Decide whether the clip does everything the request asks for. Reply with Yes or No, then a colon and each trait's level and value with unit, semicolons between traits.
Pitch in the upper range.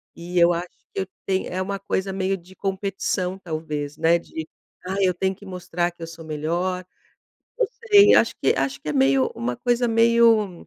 No: medium, 180 Hz